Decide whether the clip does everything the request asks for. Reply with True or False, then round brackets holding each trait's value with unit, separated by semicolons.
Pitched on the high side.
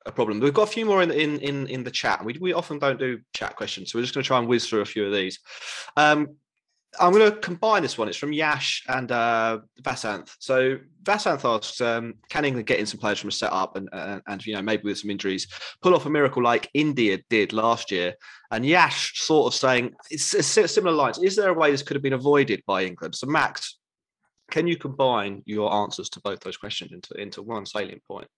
False (130 Hz)